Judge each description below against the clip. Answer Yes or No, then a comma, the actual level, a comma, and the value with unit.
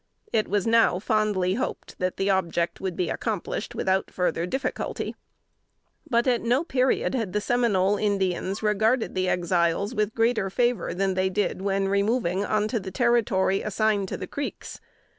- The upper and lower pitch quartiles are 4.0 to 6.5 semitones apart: No, average, 3.4 semitones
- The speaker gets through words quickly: No, average, 160 wpm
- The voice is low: No, high, 200 Hz